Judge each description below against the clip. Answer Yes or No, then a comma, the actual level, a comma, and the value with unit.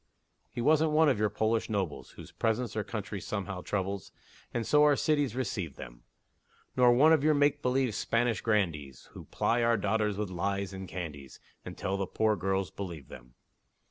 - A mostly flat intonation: No, average, 4.3 semitones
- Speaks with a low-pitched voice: Yes, low, 105 Hz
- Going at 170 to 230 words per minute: Yes, average, 175 wpm